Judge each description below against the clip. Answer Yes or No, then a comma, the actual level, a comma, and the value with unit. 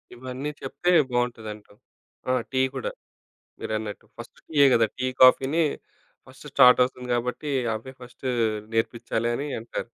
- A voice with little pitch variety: Yes, narrow, 2.3 semitones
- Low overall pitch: Yes, low, 125 Hz